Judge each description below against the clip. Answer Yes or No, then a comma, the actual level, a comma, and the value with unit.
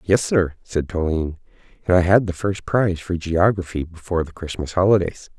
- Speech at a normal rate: Yes, average, 180 wpm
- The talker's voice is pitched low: Yes, very low, 90 Hz